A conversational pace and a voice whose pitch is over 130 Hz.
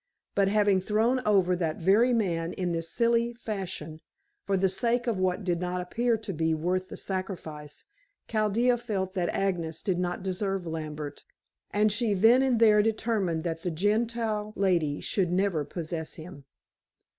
Yes: average, 160 wpm; high, 190 Hz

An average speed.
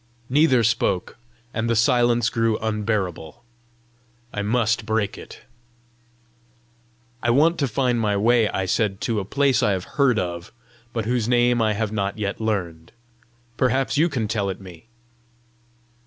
Yes: average, 150 wpm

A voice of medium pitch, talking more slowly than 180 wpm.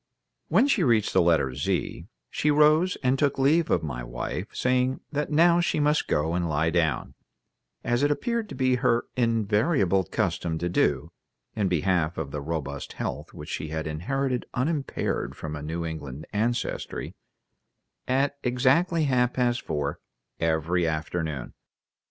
No: low, 110 Hz; average, 150 wpm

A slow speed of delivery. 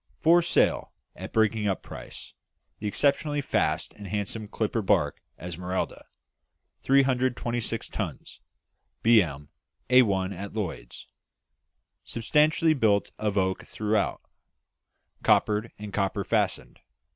Yes: slow, 100 wpm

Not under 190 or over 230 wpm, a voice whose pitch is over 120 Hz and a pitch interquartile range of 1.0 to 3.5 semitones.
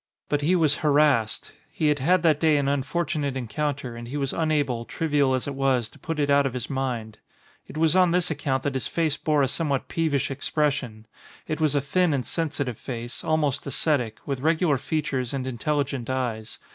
Yes: average, 200 wpm; medium, 140 Hz; average, 3.0 semitones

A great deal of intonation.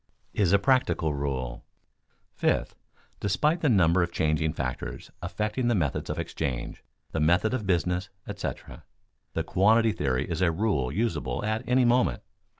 Yes: wide, 6.4 semitones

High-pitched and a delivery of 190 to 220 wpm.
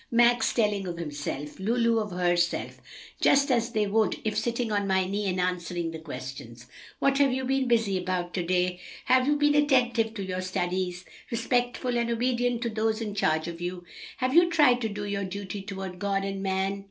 Yes: high, 205 Hz; average, 195 wpm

